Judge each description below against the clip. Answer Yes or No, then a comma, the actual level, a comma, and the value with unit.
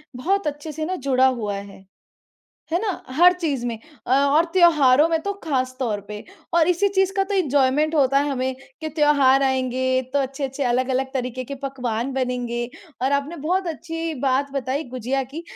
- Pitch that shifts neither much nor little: Yes, average, 3.9 semitones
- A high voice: Yes, very high, 275 Hz